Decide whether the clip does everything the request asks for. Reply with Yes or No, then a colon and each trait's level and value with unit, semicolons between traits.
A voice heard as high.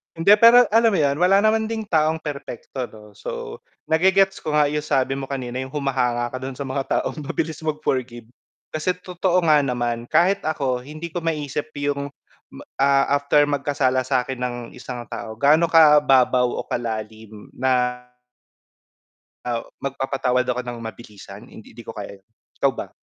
No: medium, 140 Hz